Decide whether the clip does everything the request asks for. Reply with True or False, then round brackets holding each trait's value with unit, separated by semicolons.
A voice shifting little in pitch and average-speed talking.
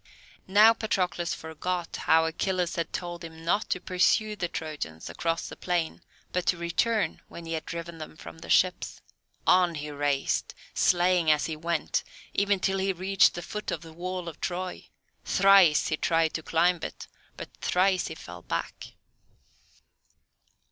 True (2.3 semitones; 160 wpm)